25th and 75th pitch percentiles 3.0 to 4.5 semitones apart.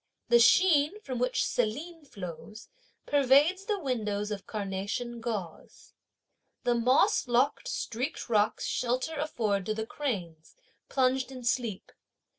No: average, 5.0 semitones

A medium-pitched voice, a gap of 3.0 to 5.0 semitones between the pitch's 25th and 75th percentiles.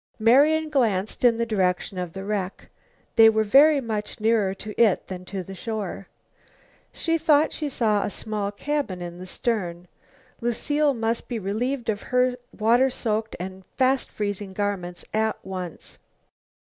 No: high, 215 Hz; average, 4.3 semitones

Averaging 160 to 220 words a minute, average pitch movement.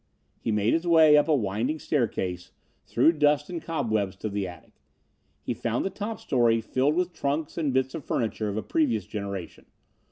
No: average, 185 wpm; wide, 6.8 semitones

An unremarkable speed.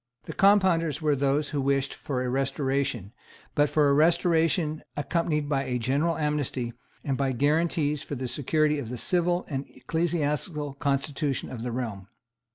Yes: average, 160 wpm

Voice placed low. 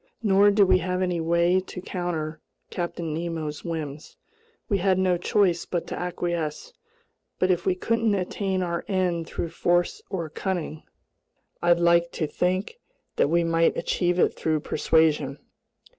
No: medium, 175 Hz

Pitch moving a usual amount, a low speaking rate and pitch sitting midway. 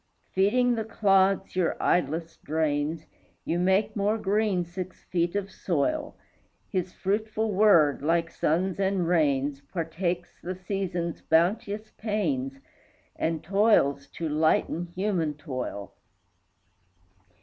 Yes: average, 3.8 semitones; slow, 110 wpm; medium, 180 Hz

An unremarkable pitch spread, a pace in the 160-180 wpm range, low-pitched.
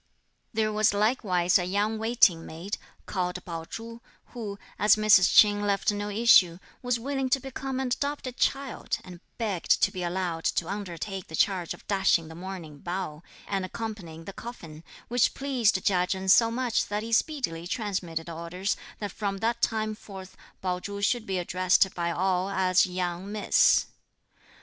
No: average, 3.8 semitones; average, 165 wpm; high, 195 Hz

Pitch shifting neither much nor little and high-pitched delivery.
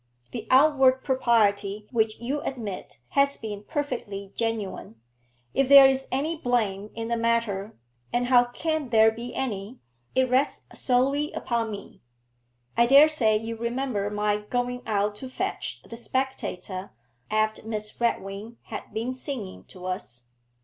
Yes: average, 3.8 semitones; high, 230 Hz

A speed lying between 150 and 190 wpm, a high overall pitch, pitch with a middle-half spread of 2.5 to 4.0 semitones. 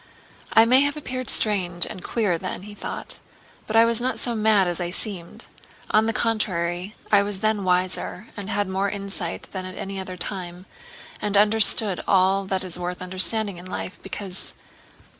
Yes: average, 180 wpm; high, 195 Hz; average, 2.9 semitones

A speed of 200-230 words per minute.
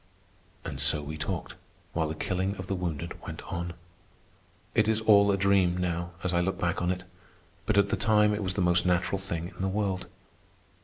Yes: fast, 205 wpm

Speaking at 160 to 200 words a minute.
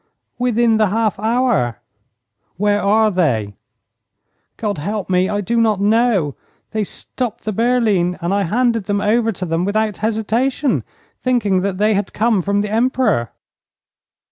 No: average, 145 wpm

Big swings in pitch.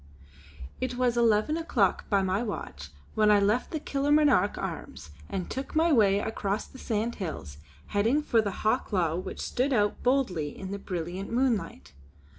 No: average, 4.7 semitones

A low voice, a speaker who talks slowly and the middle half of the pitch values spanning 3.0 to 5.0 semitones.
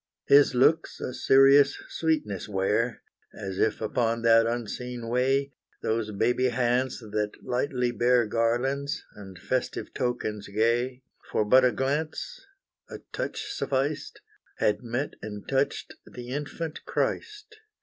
Yes: low, 125 Hz; slow, 125 wpm; average, 3.4 semitones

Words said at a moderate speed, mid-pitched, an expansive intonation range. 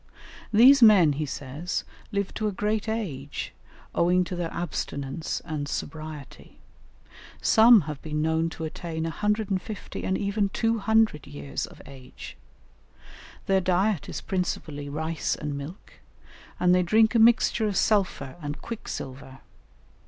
No: slow, 130 wpm; medium, 175 Hz; wide, 5.7 semitones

